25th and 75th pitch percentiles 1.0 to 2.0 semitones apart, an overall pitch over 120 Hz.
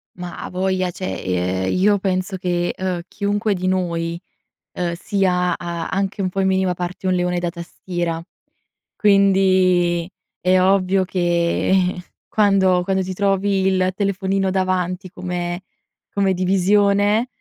Yes: narrow, 1.6 semitones; medium, 185 Hz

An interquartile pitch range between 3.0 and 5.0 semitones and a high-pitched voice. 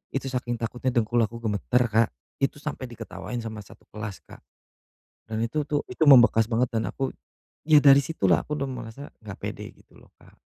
No: average, 3.5 semitones; low, 120 Hz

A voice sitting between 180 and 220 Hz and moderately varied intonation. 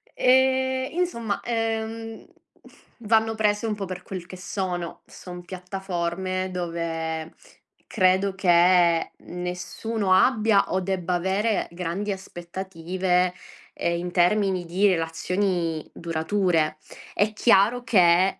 Yes: medium, 185 Hz; average, 3.1 semitones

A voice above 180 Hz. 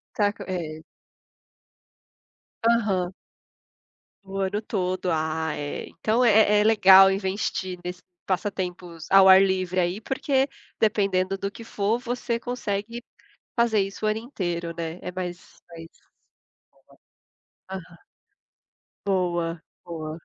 Yes: high, 190 Hz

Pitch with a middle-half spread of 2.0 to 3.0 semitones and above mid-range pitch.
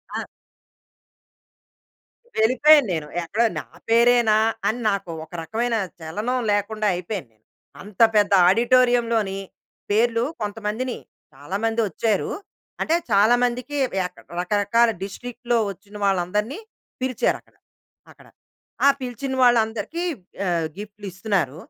No: average, 3.5 semitones; high, 215 Hz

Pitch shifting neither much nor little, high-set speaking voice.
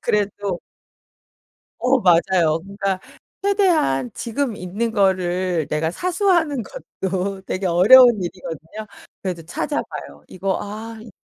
Yes: average, 4.7 semitones; high, 195 Hz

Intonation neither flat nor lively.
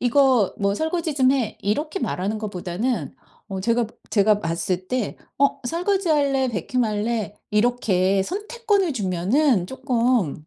No: wide, 6.0 semitones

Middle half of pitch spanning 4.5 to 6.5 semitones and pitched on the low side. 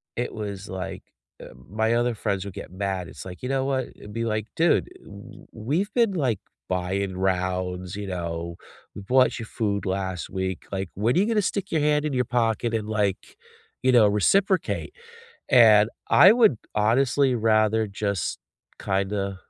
Yes: average, 4.8 semitones; low, 105 Hz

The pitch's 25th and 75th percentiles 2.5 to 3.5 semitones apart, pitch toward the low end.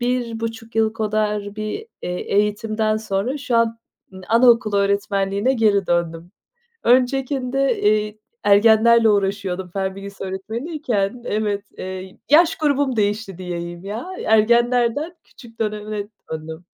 No: average, 3.1 semitones; high, 215 Hz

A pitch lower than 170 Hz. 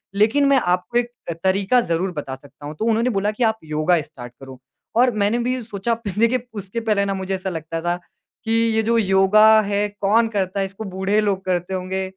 No: high, 200 Hz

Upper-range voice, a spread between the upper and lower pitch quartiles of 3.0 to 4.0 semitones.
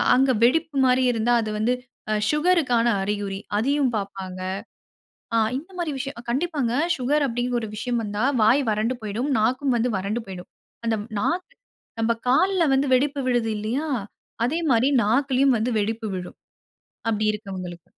No: high, 240 Hz; average, 4.4 semitones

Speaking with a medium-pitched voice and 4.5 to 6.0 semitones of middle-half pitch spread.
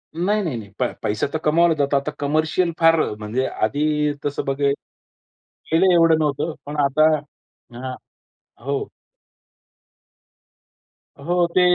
No: medium, 150 Hz; average, 3.2 semitones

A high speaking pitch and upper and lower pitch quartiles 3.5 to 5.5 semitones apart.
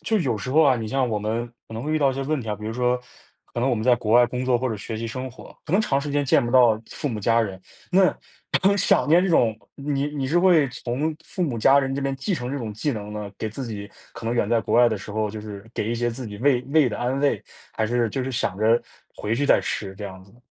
No: low, 120 Hz; average, 4.0 semitones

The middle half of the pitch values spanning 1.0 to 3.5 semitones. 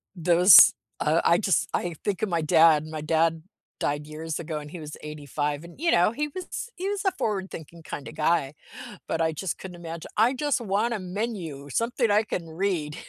No: average, 5.0 semitones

